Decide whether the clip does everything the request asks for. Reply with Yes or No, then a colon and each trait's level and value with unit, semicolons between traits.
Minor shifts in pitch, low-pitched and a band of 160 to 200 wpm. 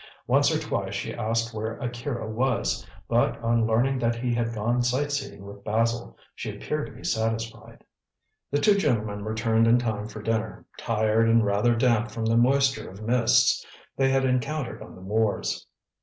Yes: narrow, 1.9 semitones; low, 115 Hz; average, 170 wpm